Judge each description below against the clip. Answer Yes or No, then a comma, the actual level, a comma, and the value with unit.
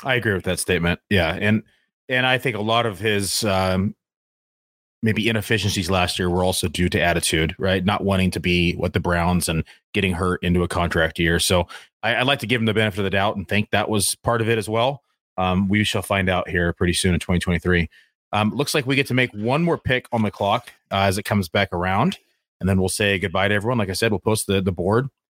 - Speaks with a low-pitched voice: Yes, low, 100 Hz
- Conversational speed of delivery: No, fast, 245 wpm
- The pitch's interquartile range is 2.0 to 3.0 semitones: No, average, 3.4 semitones